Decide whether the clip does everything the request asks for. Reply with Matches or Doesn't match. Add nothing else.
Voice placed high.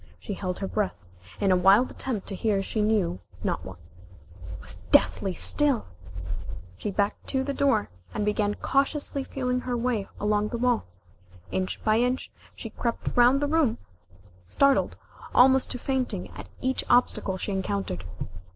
Matches